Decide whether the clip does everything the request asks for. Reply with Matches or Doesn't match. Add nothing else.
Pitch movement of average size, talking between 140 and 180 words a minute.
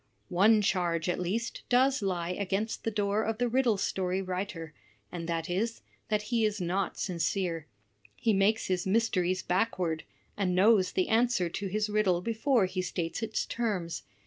Matches